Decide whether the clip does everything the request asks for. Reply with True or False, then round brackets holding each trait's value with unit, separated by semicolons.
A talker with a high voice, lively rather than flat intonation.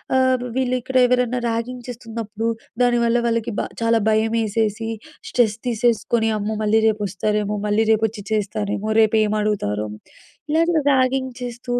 False (225 Hz; 2.5 semitones)